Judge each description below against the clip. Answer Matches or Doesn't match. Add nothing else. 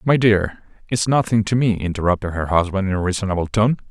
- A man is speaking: Matches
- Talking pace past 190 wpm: Matches